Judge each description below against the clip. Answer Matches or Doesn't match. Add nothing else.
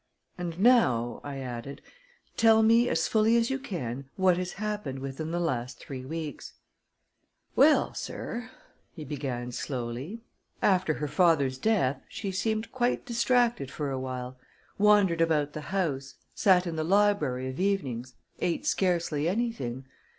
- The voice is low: Doesn't match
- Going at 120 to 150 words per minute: Matches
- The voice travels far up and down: Matches